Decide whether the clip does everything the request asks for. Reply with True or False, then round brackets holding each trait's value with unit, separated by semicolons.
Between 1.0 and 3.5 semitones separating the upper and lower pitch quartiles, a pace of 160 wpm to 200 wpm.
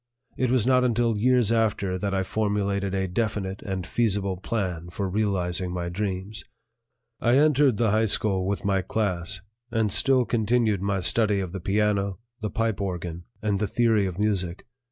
True (2.9 semitones; 170 wpm)